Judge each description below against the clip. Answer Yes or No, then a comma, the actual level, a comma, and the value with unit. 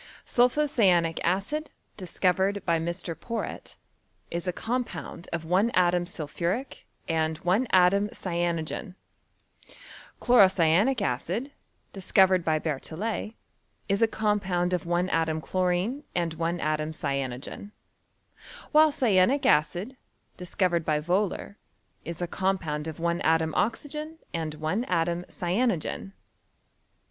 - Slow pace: Yes, slow, 115 wpm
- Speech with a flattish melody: No, average, 3.9 semitones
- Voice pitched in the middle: Yes, medium, 180 Hz